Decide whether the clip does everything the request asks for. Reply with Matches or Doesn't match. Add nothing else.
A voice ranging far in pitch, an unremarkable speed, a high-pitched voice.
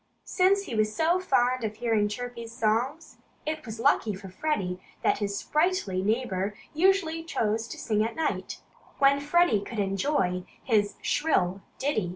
Matches